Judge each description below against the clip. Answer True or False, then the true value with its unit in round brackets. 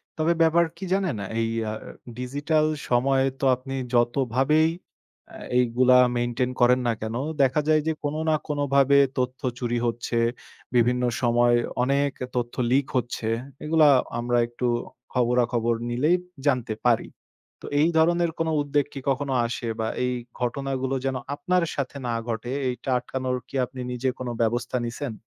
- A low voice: True (130 Hz)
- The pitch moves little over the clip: False (3.0 semitones)